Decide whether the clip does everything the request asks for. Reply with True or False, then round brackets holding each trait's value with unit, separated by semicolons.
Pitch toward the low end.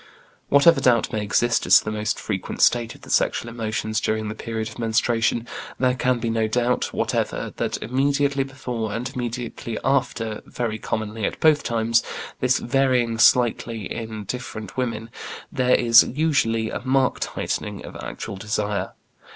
True (115 Hz)